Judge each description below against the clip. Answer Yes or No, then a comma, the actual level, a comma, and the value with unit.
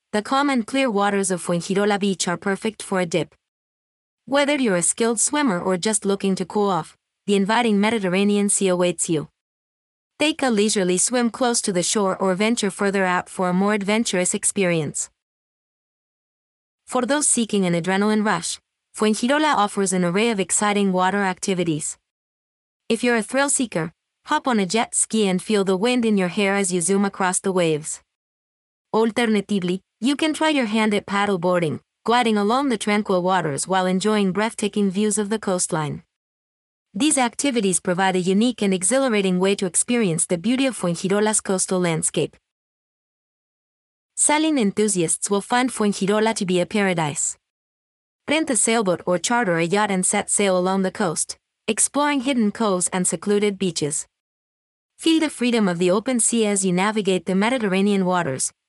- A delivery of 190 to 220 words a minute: No, average, 165 wpm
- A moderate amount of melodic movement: Yes, average, 3.6 semitones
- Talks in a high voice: Yes, high, 200 Hz